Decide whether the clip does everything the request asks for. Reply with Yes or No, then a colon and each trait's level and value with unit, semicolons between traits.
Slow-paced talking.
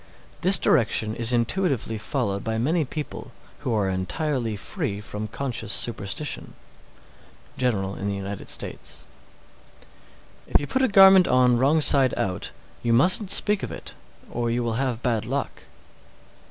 No: average, 150 wpm